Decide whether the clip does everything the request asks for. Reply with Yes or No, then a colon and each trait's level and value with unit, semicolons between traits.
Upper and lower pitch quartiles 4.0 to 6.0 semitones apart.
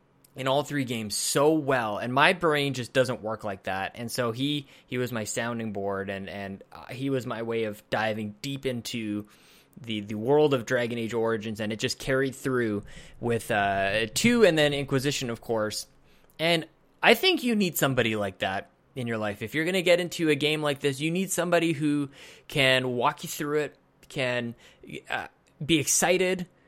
Yes: average, 5.0 semitones